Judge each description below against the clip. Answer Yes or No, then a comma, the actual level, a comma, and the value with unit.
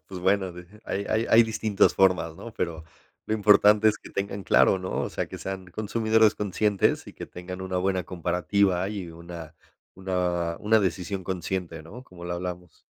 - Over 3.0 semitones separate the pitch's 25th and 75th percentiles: No, average, 2.7 semitones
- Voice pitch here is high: No, very low, 95 Hz